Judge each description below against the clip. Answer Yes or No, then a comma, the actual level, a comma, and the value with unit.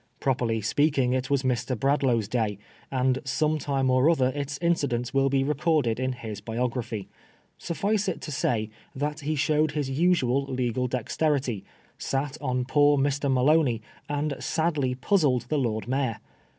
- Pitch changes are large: No, average, 2.8 semitones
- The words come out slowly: No, average, 150 wpm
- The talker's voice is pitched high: No, low, 135 Hz